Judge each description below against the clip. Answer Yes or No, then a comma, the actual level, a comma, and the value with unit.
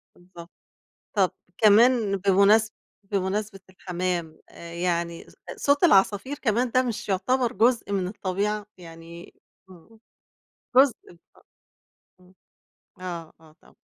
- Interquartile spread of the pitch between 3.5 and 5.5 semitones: Yes, average, 3.9 semitones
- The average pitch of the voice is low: No, high, 195 Hz